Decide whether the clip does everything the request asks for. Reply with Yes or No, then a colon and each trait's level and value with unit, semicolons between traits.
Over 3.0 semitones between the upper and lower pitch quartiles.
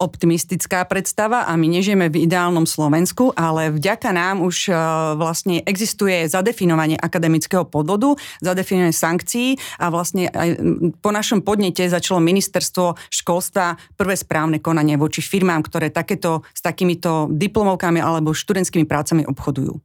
No: average, 2.7 semitones